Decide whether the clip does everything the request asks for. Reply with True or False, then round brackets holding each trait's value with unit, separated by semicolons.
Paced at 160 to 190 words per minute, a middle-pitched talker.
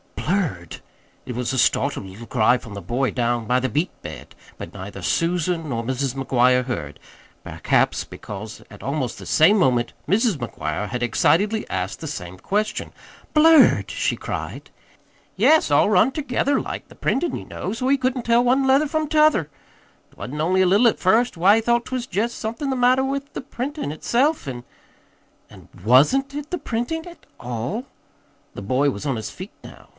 True (185 wpm; 180 Hz)